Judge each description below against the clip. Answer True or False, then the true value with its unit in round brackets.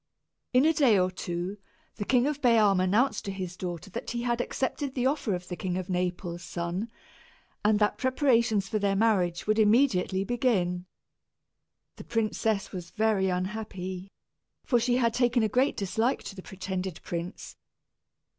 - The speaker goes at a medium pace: True (165 wpm)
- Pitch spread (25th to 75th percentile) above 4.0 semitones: True (4.6 semitones)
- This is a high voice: True (205 Hz)